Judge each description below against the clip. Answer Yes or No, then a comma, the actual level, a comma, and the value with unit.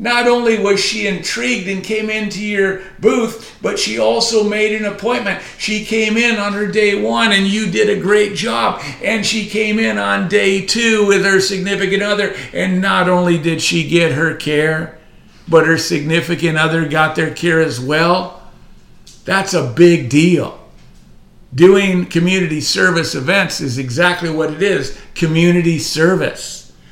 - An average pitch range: Yes, average, 4.2 semitones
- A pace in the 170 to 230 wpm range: No, average, 160 wpm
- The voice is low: No, medium, 185 Hz